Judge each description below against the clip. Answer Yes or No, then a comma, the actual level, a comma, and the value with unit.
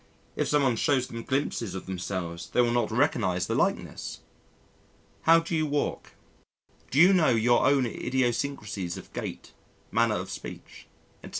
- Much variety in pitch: Yes, wide, 6.0 semitones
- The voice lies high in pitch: No, low, 120 Hz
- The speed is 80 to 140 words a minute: No, average, 155 wpm